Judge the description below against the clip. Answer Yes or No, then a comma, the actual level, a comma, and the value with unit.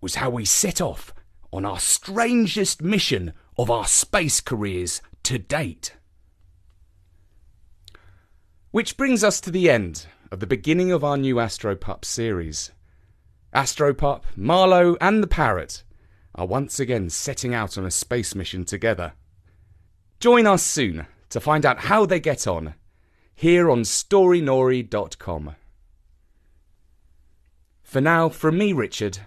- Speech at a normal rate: No, slow, 125 wpm